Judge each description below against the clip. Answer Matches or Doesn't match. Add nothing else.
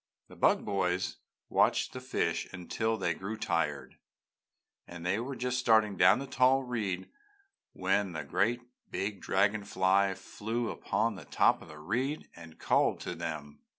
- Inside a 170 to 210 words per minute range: Doesn't match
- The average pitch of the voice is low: Matches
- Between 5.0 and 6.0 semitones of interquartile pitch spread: Doesn't match